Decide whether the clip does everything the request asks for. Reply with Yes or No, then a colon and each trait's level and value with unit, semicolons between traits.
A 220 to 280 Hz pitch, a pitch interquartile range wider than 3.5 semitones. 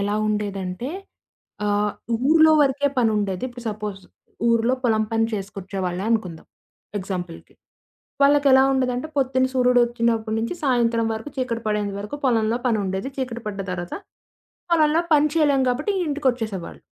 Yes: high, 230 Hz; average, 4.1 semitones